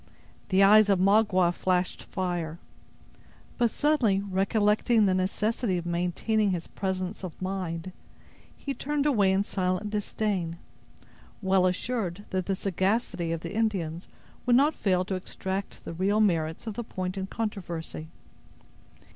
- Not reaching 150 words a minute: Yes, average, 140 wpm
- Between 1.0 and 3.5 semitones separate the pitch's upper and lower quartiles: Yes, average, 2.8 semitones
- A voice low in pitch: No, high, 190 Hz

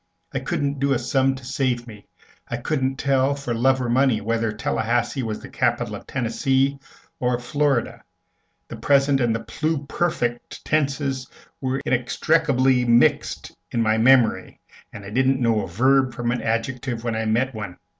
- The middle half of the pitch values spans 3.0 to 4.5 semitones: No, narrow, 2.6 semitones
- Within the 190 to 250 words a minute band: No, average, 165 wpm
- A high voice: No, low, 130 Hz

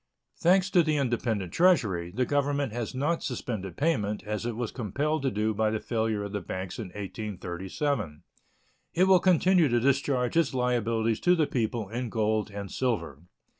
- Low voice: Yes, low, 120 Hz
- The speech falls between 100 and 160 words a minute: No, average, 170 wpm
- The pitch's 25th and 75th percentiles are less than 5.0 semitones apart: No, average, 5.3 semitones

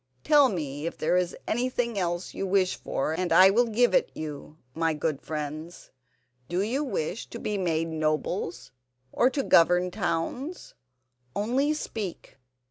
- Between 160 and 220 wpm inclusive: No, average, 150 wpm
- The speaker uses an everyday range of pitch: No, wide, 6.5 semitones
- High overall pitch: No, medium, 180 Hz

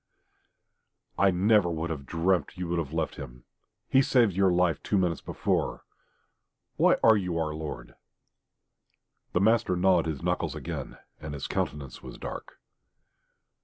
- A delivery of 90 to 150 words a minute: Yes, average, 145 wpm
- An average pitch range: Yes, average, 3.7 semitones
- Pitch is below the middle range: Yes, very low, 85 Hz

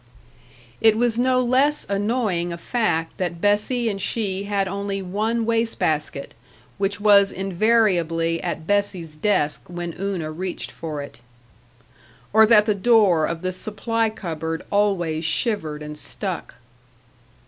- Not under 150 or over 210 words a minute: No, slow, 135 wpm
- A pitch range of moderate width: Yes, average, 4.6 semitones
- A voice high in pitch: Yes, high, 200 Hz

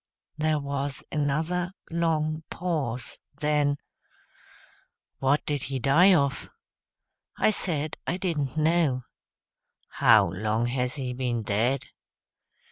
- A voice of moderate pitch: Yes, medium, 145 Hz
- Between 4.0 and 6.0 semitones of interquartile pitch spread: No, average, 3.5 semitones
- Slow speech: Yes, slow, 105 wpm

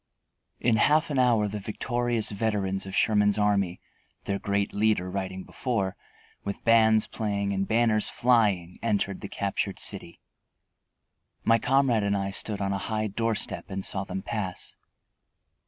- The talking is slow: No, average, 150 wpm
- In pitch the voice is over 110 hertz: No, low, 105 Hz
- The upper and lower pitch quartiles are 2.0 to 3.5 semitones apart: Yes, narrow, 2.6 semitones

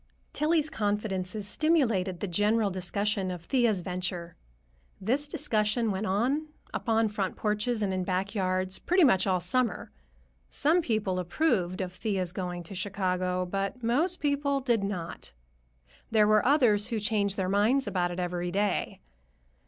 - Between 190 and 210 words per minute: No, average, 145 wpm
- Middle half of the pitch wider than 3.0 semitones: Yes, average, 4.4 semitones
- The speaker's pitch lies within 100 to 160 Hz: No, high, 205 Hz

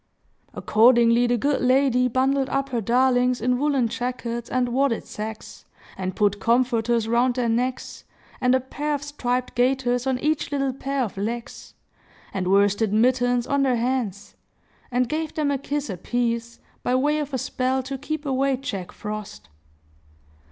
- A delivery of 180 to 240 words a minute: No, average, 160 wpm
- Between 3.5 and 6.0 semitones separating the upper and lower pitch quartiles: No, narrow, 2.5 semitones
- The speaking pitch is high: Yes, very high, 250 Hz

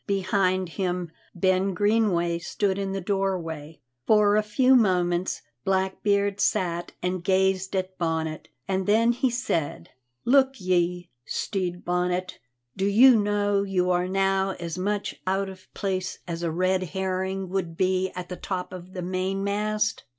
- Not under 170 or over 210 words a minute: No, average, 145 wpm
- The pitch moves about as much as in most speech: No, narrow, 2.0 semitones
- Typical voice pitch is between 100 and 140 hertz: No, high, 190 Hz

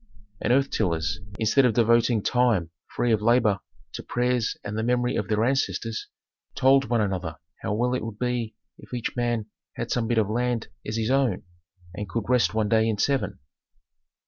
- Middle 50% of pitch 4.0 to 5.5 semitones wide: No, narrow, 2.4 semitones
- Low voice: Yes, low, 115 Hz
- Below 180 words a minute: No, average, 185 wpm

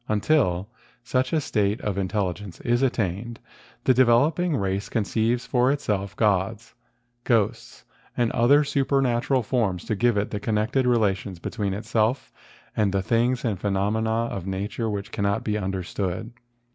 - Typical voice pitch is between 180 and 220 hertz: No, low, 110 Hz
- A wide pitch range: No, average, 3.5 semitones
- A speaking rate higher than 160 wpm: No, average, 145 wpm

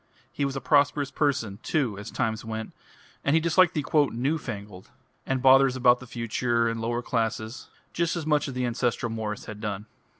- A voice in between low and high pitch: No, low, 125 Hz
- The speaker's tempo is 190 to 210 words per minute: Yes, average, 195 wpm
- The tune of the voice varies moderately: Yes, average, 3.9 semitones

